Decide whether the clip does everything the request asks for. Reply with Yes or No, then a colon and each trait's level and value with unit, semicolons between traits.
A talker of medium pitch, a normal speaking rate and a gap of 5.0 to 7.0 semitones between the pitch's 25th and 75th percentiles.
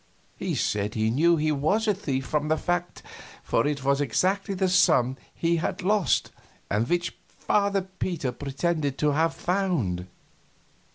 Yes: medium, 155 Hz; average, 155 wpm; average, 5.3 semitones